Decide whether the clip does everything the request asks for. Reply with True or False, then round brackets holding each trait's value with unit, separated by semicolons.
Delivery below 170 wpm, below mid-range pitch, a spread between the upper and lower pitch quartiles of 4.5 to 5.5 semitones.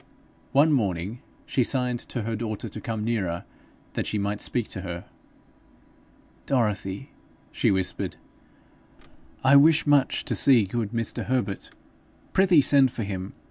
True (140 wpm; 115 Hz; 4.9 semitones)